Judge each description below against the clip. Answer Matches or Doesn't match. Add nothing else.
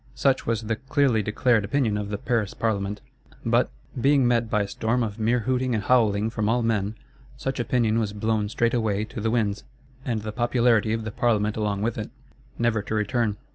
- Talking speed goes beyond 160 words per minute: Matches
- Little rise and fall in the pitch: Matches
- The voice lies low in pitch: Matches